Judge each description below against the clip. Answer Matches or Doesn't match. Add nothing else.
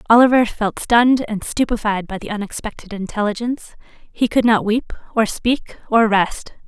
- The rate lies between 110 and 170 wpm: Matches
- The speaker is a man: Doesn't match